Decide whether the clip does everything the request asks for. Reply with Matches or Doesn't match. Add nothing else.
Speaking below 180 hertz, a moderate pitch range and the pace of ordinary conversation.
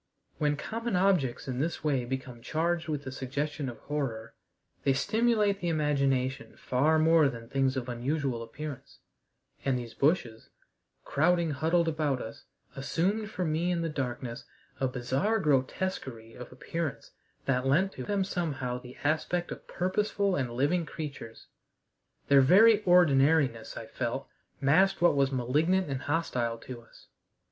Matches